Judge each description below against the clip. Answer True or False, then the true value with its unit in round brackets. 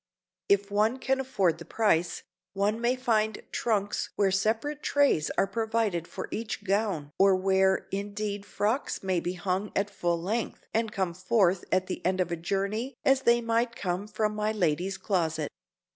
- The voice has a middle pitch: False (200 Hz)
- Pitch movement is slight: False (3.1 semitones)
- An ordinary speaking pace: True (170 wpm)